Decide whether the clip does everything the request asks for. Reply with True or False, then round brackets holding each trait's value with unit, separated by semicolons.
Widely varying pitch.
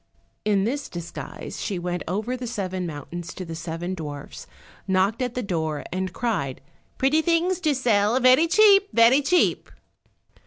True (7.0 semitones)